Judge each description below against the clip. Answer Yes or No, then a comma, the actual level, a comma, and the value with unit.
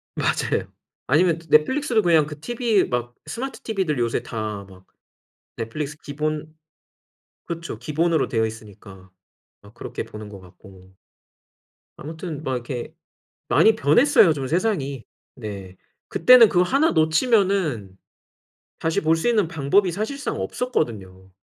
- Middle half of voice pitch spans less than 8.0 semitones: No, wide, 8.8 semitones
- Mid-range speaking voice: Yes, medium, 155 Hz